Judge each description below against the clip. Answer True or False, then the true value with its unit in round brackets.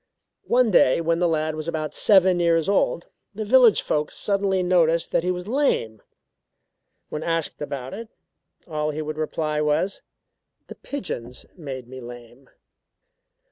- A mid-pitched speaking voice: True (165 Hz)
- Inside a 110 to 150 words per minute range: True (145 wpm)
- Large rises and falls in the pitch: False (3.8 semitones)